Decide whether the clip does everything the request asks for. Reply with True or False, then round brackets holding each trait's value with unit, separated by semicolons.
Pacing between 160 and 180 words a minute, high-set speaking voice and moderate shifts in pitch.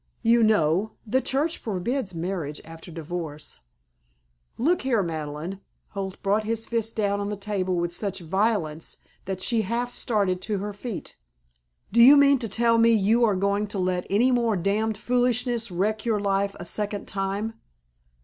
True (165 wpm; 205 Hz; 3.7 semitones)